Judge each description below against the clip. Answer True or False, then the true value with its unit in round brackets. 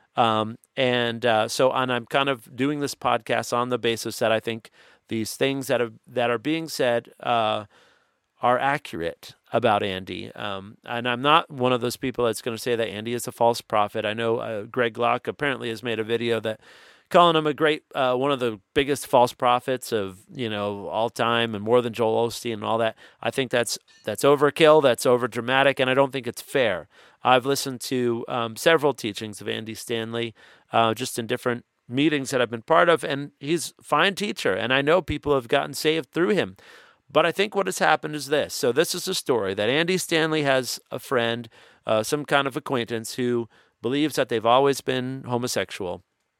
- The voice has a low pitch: True (125 Hz)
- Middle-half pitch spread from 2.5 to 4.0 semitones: True (3.5 semitones)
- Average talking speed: False (210 wpm)